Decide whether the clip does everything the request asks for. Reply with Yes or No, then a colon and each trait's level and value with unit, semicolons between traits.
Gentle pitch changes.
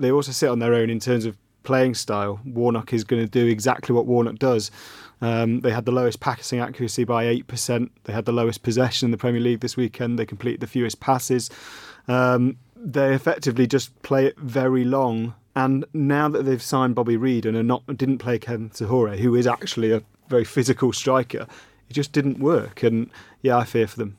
Yes: narrow, 2.1 semitones